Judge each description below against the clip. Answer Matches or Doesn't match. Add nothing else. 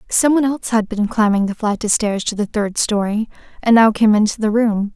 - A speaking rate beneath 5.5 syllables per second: Doesn't match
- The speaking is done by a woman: Matches